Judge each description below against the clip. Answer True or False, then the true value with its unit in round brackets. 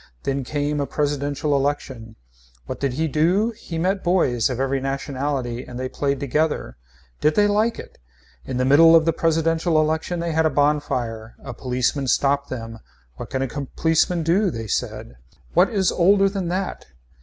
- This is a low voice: False (145 Hz)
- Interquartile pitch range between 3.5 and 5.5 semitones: True (3.9 semitones)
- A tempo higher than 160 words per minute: True (175 wpm)